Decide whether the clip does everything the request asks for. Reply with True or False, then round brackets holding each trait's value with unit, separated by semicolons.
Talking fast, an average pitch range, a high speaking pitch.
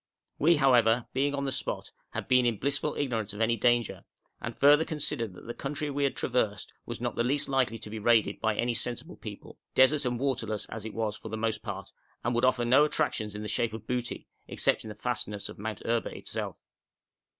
False (215 wpm; 3.6 semitones; 120 Hz)